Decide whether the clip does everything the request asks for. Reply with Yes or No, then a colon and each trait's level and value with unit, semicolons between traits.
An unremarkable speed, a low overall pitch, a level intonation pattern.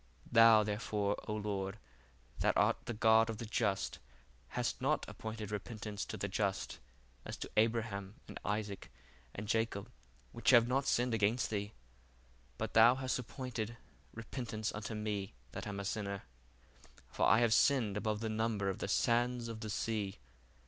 Yes: average, 160 wpm; low, 110 Hz; narrow, 2.0 semitones